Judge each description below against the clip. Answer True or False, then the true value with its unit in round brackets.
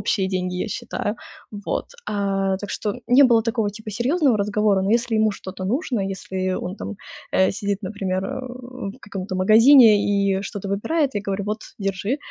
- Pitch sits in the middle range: False (205 Hz)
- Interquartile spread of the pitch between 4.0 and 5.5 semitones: False (2.7 semitones)